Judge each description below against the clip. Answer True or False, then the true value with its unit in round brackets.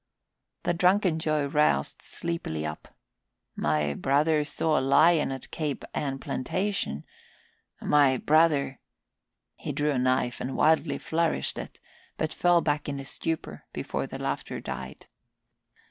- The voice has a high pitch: False (150 Hz)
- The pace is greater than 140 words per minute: False (135 wpm)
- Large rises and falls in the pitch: False (3.4 semitones)